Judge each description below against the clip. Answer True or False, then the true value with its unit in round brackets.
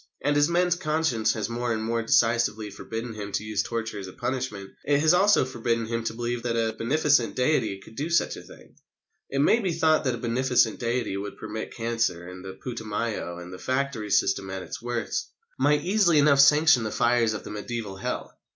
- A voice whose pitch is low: True (115 Hz)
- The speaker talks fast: True (210 wpm)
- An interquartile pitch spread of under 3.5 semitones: False (4.4 semitones)